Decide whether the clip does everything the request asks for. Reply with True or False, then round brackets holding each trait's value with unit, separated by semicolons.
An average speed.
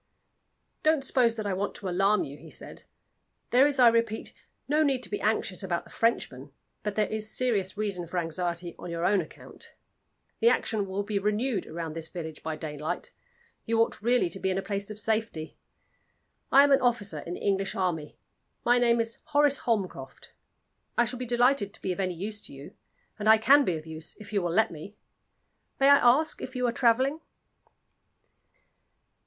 True (195 wpm)